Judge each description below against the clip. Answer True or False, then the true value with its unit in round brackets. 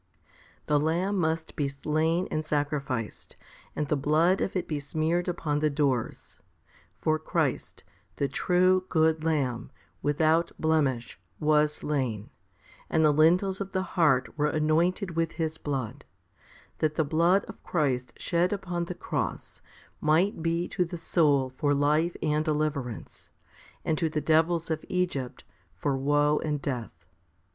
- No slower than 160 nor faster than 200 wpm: False (145 wpm)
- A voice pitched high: False (155 Hz)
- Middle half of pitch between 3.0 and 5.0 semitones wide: False (2.6 semitones)